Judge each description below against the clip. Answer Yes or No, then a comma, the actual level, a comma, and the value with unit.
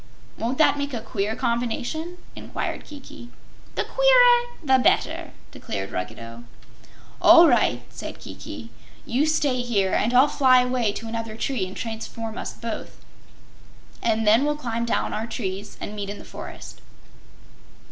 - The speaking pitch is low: No, high, 235 Hz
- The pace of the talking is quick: No, average, 145 wpm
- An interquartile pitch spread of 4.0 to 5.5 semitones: Yes, average, 4.6 semitones